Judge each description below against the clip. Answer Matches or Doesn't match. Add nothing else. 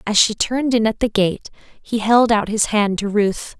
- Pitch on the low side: Doesn't match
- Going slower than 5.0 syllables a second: Matches